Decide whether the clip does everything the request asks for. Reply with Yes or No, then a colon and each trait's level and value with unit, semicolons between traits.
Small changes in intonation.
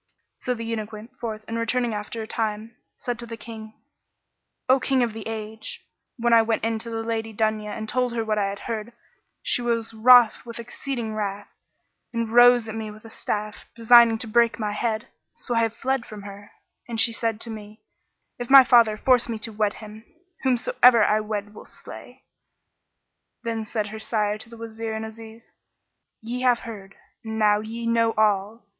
Yes: narrow, 1.5 semitones